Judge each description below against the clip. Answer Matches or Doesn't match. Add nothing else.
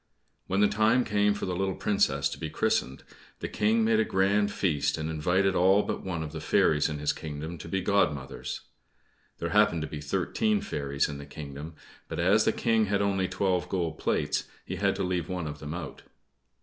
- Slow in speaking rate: Doesn't match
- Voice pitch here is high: Doesn't match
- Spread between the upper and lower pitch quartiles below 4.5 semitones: Doesn't match